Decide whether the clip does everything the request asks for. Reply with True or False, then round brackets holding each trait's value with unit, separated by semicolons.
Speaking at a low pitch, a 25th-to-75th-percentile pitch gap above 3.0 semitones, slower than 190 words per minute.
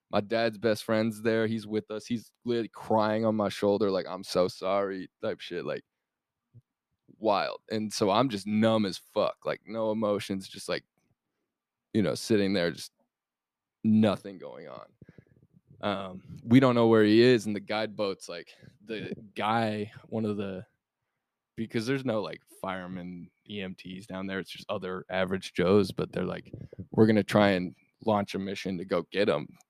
False (105 Hz; 2.7 semitones; 175 wpm)